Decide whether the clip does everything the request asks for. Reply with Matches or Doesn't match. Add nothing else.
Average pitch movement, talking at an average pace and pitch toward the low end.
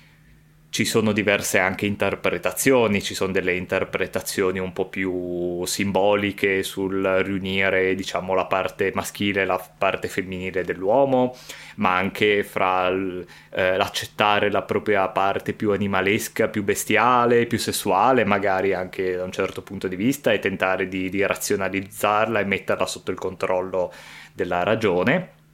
Doesn't match